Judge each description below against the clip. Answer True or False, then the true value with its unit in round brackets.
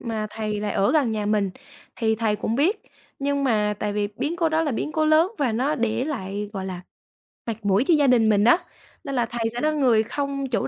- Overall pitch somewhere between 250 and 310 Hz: False (230 Hz)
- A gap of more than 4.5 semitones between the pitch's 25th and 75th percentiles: True (5.1 semitones)